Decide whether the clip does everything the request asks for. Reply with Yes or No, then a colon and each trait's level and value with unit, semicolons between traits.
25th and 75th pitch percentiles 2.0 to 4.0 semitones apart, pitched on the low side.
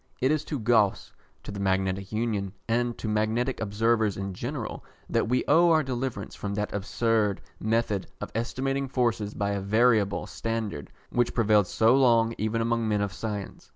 Yes: average, 2.9 semitones; low, 110 Hz